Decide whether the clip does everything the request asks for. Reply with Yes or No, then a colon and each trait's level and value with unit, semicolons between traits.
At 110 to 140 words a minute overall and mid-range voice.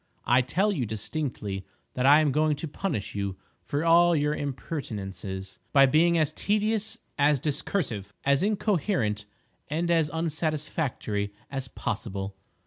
Yes: slow, 135 wpm; medium, 145 Hz